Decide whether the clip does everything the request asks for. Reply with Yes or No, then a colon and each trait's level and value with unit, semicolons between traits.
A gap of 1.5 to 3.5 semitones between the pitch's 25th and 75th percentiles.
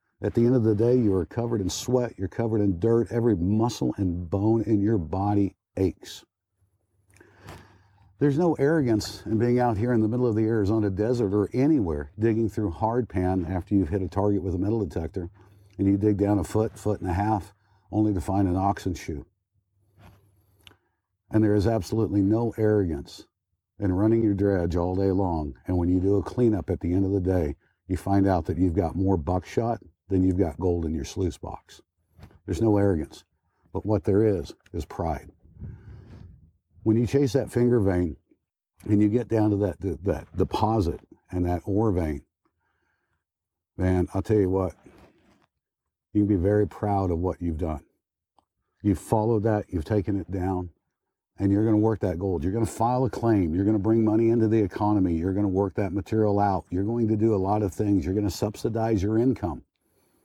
Yes: average, 2.8 semitones